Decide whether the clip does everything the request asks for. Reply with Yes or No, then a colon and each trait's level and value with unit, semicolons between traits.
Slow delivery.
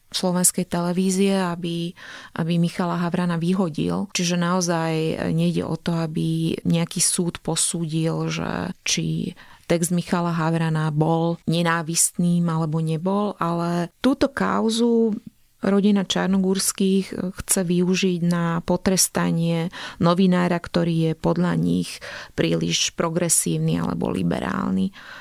Yes: slow, 100 wpm